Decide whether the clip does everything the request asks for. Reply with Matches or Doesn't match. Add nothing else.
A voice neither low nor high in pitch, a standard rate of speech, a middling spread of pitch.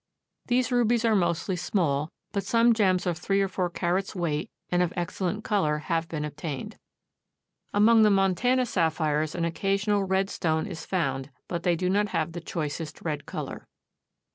Matches